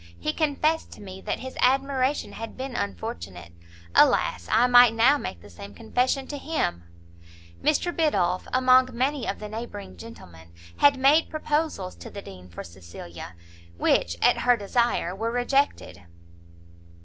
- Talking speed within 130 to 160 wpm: Yes, average, 150 wpm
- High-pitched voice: Yes, high, 240 Hz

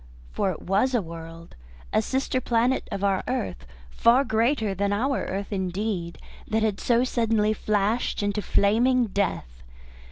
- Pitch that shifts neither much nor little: Yes, average, 3.7 semitones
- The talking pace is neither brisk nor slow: Yes, average, 150 wpm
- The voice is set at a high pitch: Yes, high, 210 Hz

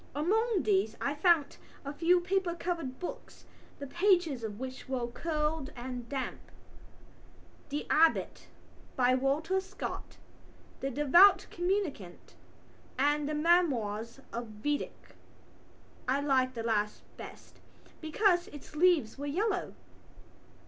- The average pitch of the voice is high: Yes, very high, 290 Hz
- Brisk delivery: No, slow, 115 wpm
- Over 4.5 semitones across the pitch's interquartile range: Yes, average, 5.3 semitones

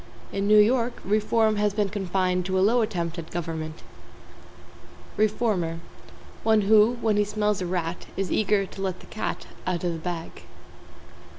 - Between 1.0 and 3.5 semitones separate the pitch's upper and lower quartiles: Yes, average, 3.1 semitones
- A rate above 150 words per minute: Yes, average, 165 wpm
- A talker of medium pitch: No, high, 195 Hz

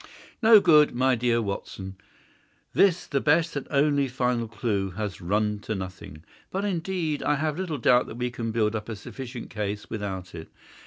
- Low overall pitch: Yes, low, 120 Hz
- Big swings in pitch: Yes, wide, 6.0 semitones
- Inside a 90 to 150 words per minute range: No, average, 175 wpm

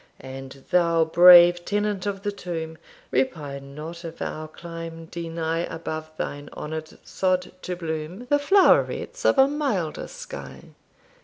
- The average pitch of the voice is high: No, medium, 170 Hz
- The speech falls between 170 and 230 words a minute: No, slow, 135 wpm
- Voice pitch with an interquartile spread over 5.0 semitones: No, average, 3.4 semitones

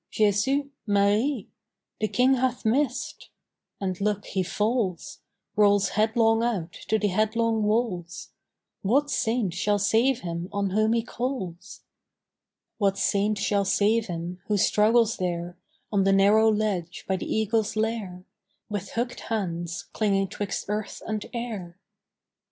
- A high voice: Yes, high, 210 Hz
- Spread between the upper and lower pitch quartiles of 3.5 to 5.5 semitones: No, average, 2.8 semitones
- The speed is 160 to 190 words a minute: No, slow, 135 wpm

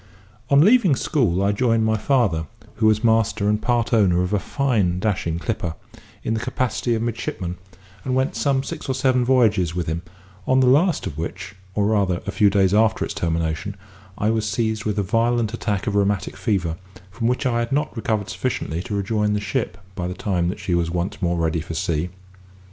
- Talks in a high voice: No, low, 105 Hz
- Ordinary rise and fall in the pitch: Yes, average, 4.6 semitones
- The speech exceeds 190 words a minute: Yes, fast, 205 wpm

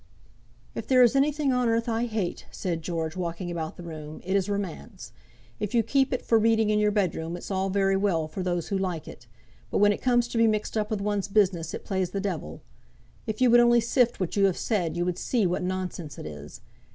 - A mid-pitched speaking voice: No, high, 195 Hz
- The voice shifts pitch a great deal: No, average, 4.4 semitones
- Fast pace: Yes, fast, 235 wpm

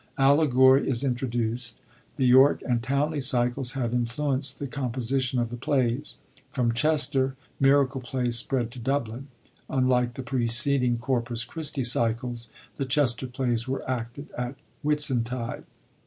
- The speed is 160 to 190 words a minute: No, average, 140 wpm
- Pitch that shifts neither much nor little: No, narrow, 2.3 semitones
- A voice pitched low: Yes, low, 130 Hz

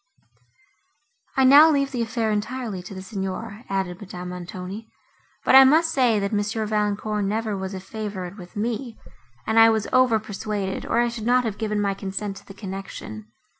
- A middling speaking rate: Yes, average, 175 wpm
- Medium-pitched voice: No, high, 210 Hz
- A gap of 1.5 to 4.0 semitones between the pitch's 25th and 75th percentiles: Yes, average, 3.0 semitones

